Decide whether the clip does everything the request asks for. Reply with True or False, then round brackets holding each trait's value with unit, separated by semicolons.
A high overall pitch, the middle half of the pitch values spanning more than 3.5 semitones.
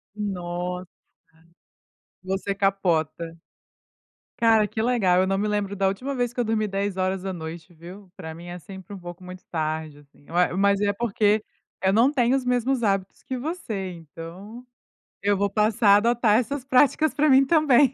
True (200 Hz; 4.7 semitones)